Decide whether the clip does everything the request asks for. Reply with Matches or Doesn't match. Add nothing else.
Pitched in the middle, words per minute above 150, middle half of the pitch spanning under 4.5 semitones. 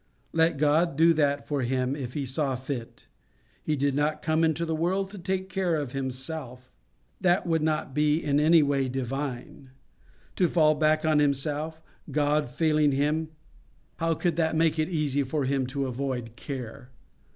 Matches